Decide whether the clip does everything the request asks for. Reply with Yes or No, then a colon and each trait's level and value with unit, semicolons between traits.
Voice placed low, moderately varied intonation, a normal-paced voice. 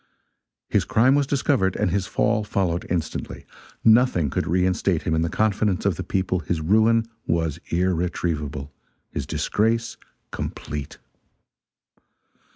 No: very low, 90 Hz; average, 4.8 semitones; slow, 125 wpm